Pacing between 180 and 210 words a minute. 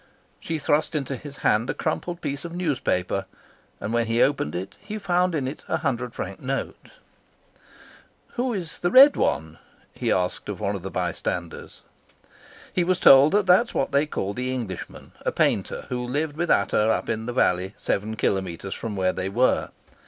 Yes: average, 185 wpm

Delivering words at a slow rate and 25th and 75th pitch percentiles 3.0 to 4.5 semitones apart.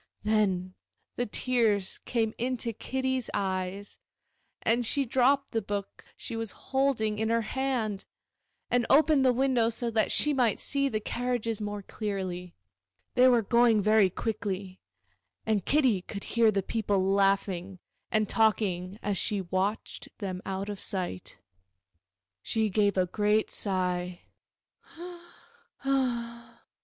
Yes: slow, 125 wpm; average, 3.6 semitones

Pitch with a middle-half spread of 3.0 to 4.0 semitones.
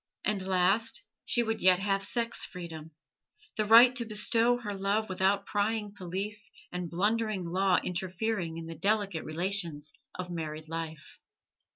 Yes: average, 3.7 semitones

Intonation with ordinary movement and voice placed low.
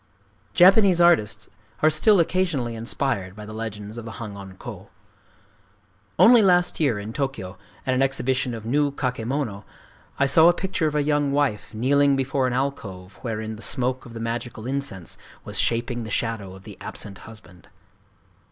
Yes: average, 4.8 semitones; low, 125 Hz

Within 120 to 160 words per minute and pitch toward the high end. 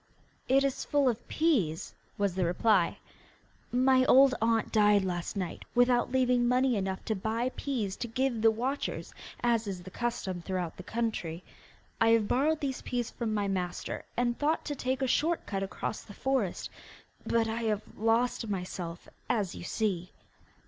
No: average, 170 wpm; high, 225 Hz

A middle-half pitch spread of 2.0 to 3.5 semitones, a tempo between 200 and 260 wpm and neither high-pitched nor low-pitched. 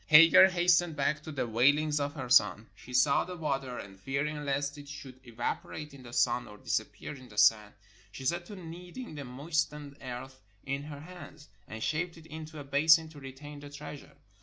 Yes: average, 3.2 semitones; fast, 205 wpm; medium, 145 Hz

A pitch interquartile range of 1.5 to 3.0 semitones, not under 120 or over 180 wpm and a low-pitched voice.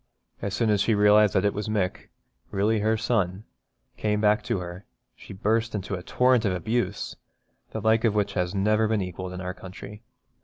No: narrow, 2.5 semitones; average, 195 wpm; low, 105 Hz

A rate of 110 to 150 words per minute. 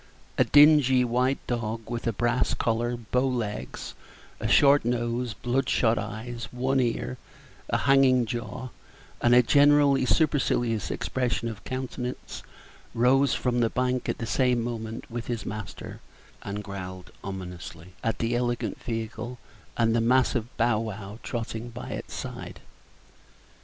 Yes: slow, 135 wpm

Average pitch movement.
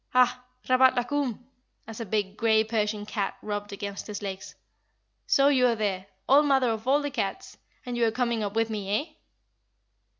Yes: average, 3.5 semitones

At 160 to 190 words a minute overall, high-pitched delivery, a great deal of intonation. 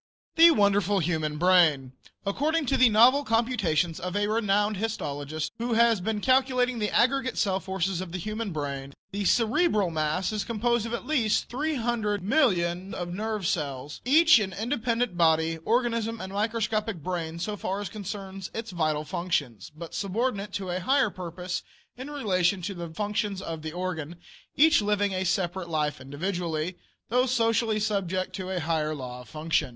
No: average, 165 wpm; high, 195 Hz; average, 4.9 semitones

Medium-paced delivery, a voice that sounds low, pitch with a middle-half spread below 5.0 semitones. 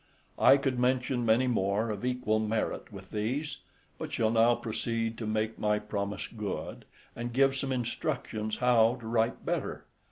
Yes: average, 160 wpm; low, 115 Hz; narrow, 2.5 semitones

